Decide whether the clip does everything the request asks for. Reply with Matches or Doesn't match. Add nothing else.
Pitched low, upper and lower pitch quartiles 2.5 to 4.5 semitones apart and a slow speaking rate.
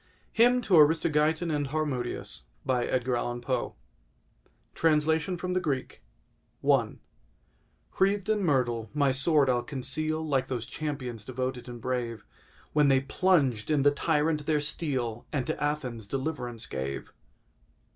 Doesn't match